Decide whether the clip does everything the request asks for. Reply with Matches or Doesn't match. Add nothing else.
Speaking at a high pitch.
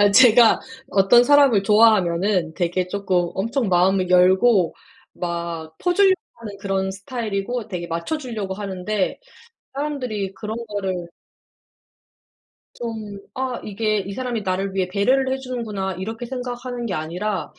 Matches